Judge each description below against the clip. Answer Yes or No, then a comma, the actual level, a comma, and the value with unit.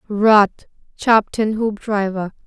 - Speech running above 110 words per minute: No, slow, 95 wpm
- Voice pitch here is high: Yes, high, 210 Hz